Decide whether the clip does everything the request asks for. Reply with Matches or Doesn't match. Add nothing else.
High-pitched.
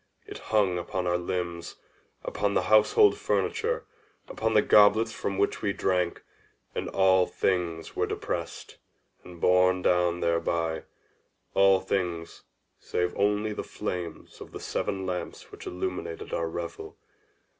Doesn't match